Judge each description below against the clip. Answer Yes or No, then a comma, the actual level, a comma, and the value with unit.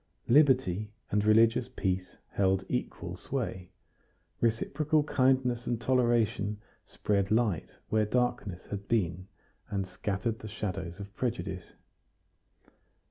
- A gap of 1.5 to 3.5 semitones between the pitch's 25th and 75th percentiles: No, average, 3.9 semitones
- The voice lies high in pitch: No, low, 105 Hz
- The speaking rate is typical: No, slow, 105 wpm